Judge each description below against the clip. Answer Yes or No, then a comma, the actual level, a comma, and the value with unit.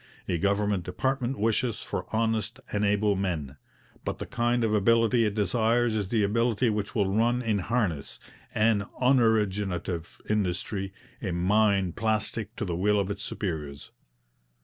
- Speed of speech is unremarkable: Yes, average, 150 wpm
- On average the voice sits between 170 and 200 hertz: No, low, 105 Hz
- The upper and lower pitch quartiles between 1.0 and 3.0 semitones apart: Yes, average, 2.7 semitones